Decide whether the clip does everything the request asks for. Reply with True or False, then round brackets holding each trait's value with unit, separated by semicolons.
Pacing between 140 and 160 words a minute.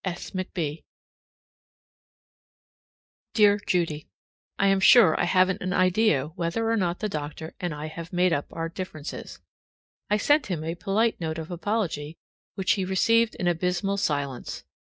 True (150 wpm)